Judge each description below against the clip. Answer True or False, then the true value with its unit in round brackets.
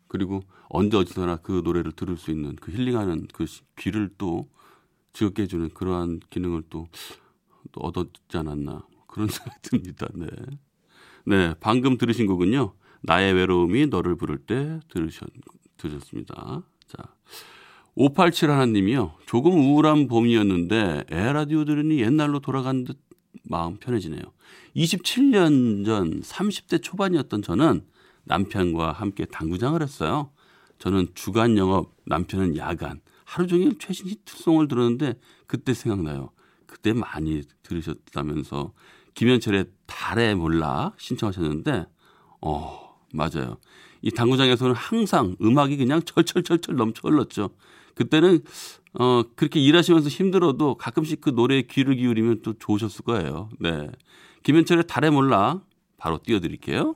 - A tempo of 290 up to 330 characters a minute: True (295 characters per minute)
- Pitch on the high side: False (115 Hz)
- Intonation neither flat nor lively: False (8.5 semitones)